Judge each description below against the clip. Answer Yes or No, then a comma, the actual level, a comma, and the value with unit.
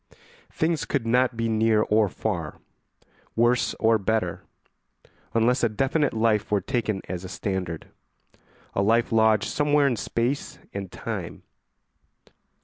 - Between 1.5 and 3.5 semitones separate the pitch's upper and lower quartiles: Yes, average, 3.0 semitones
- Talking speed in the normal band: No, slow, 130 wpm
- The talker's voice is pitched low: Yes, low, 115 Hz